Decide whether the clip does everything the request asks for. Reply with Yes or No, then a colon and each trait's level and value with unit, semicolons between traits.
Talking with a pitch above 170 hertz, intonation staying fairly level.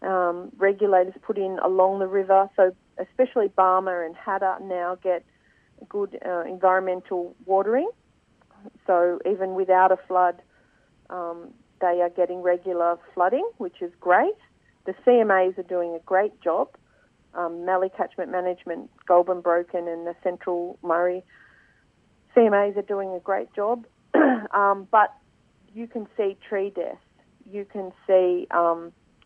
Yes: medium, 185 Hz; narrow, 2.1 semitones